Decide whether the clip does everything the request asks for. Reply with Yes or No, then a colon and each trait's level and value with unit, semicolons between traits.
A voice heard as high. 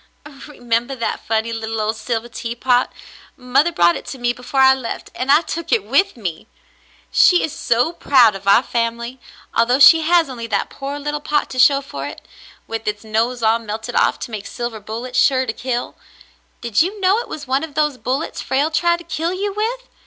Yes: very high, 250 Hz